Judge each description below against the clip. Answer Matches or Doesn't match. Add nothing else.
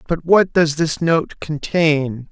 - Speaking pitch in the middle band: Matches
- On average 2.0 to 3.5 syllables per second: Matches